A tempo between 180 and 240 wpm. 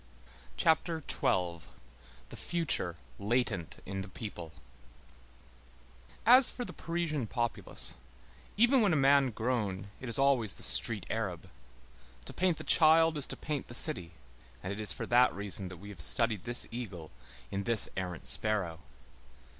No: average, 145 wpm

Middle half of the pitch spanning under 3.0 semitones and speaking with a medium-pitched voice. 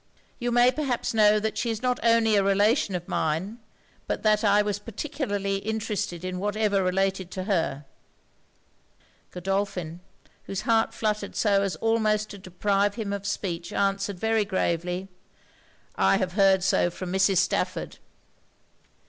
No: narrow, 2.5 semitones; high, 200 Hz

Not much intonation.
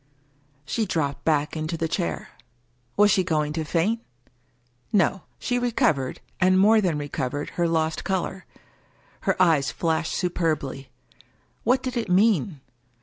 No: average, 4.3 semitones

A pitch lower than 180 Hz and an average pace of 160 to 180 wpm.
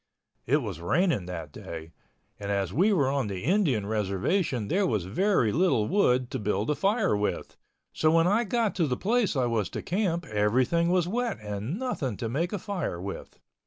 No: low, 135 Hz; average, 195 wpm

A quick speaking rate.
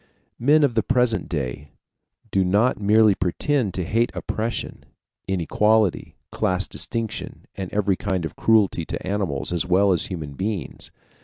No: average, 145 wpm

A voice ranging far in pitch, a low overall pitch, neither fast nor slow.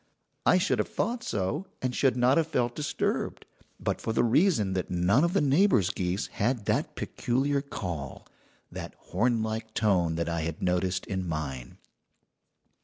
Yes: wide, 7.4 semitones; low, 110 Hz; average, 160 wpm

